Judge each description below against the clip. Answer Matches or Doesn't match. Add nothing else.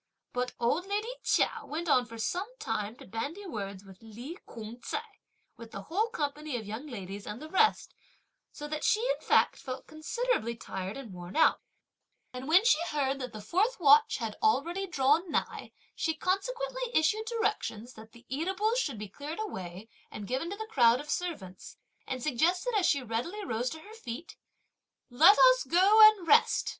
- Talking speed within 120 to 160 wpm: Doesn't match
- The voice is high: Matches